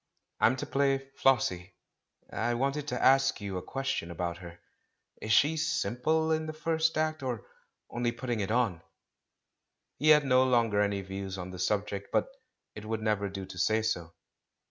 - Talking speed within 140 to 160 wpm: No, average, 175 wpm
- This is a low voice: Yes, low, 115 Hz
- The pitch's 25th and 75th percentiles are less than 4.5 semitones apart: No, wide, 5.6 semitones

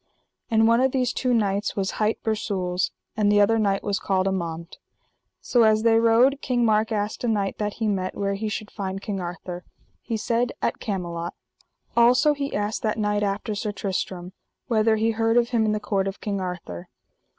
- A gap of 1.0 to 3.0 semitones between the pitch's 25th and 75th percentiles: Yes, narrow, 2.6 semitones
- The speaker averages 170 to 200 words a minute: Yes, average, 195 wpm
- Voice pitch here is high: Yes, high, 210 Hz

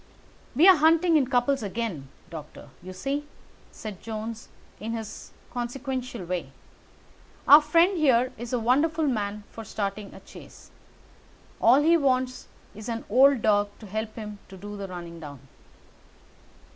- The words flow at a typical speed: Yes, average, 145 wpm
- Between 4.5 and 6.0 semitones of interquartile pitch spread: Yes, average, 5.0 semitones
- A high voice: Yes, high, 230 Hz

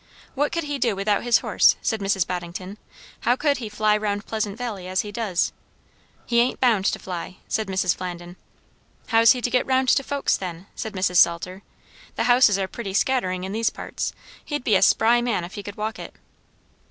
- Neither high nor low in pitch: No, high, 210 Hz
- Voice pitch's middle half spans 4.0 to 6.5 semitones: Yes, average, 4.3 semitones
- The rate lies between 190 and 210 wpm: Yes, average, 200 wpm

